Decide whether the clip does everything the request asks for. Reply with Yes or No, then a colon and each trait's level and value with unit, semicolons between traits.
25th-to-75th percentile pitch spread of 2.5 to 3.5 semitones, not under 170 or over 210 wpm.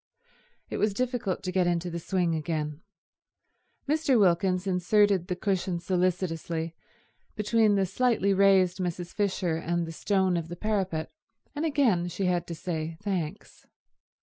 No: average, 2.9 semitones; average, 145 wpm